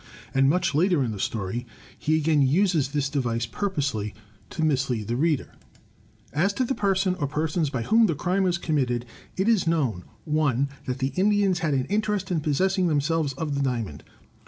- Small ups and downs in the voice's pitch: No, wide, 5.6 semitones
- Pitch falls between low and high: Yes, medium, 150 Hz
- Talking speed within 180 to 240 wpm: Yes, average, 190 wpm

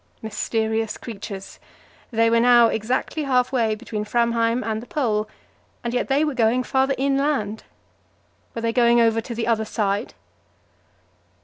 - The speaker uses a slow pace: No, average, 145 wpm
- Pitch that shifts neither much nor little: No, narrow, 2.2 semitones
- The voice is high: Yes, high, 230 Hz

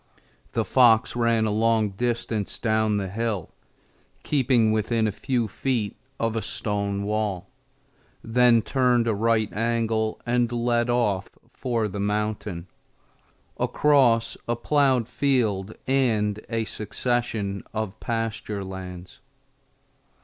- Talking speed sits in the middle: No, slow, 115 wpm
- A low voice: Yes, low, 115 Hz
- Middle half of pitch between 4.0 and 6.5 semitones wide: No, narrow, 2.4 semitones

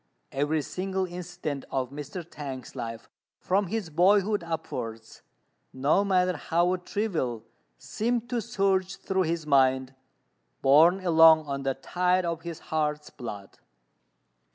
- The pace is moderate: No, slow, 125 wpm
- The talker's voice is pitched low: No, medium, 165 Hz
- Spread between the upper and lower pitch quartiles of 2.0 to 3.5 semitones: No, average, 5.2 semitones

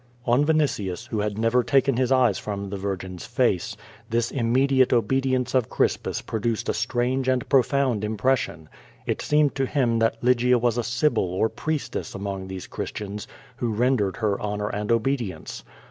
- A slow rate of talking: No, average, 165 wpm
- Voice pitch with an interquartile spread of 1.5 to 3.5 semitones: No, average, 3.9 semitones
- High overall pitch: No, low, 120 Hz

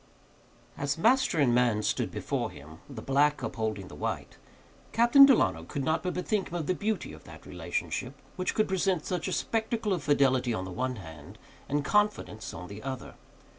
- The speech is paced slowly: No, average, 185 wpm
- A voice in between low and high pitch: Yes, medium, 145 Hz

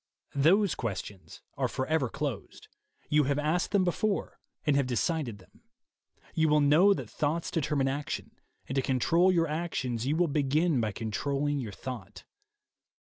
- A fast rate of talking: No, average, 155 wpm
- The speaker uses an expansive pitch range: No, average, 3.9 semitones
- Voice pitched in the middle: Yes, medium, 145 Hz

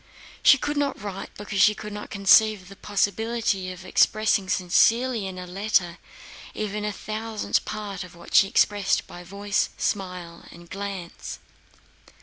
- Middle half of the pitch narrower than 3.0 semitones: Yes, narrow, 2.5 semitones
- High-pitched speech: Yes, high, 200 Hz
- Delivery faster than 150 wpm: No, average, 145 wpm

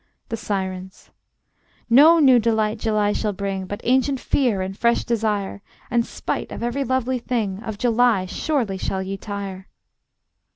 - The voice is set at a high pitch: Yes, high, 220 Hz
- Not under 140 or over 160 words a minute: Yes, average, 150 wpm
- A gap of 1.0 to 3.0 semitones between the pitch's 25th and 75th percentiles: No, average, 3.8 semitones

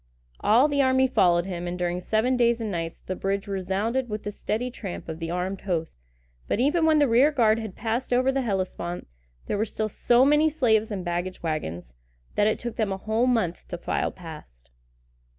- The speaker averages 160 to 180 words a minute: No, fast, 205 wpm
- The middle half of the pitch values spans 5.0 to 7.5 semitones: Yes, wide, 5.6 semitones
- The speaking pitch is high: Yes, high, 210 Hz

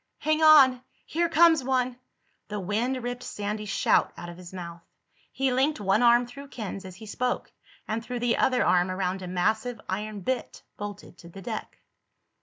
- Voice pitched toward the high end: Yes, high, 225 Hz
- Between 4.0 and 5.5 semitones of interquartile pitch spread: Yes, average, 4.9 semitones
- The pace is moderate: Yes, average, 180 wpm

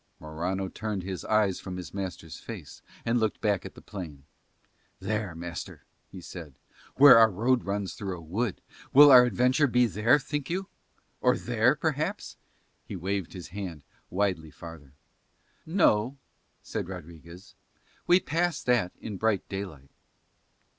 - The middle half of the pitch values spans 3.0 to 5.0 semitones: No, wide, 5.5 semitones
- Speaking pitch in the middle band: No, low, 100 Hz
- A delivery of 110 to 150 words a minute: Yes, average, 145 wpm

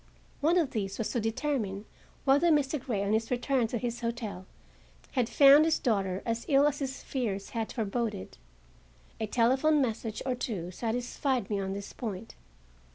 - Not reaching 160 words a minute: No, average, 165 wpm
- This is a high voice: Yes, high, 235 Hz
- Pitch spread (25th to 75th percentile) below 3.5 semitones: No, average, 4.3 semitones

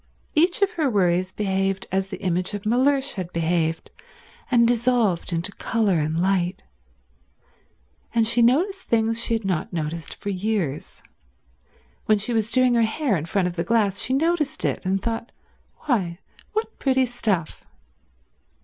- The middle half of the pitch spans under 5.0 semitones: No, wide, 5.4 semitones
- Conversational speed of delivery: Yes, average, 150 wpm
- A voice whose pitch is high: Yes, high, 205 Hz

